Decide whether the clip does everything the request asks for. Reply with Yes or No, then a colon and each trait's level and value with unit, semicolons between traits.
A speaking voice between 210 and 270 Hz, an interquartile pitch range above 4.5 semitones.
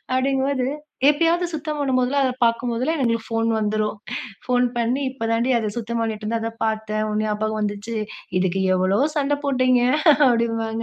No: high, 230 Hz; average, 3.2 semitones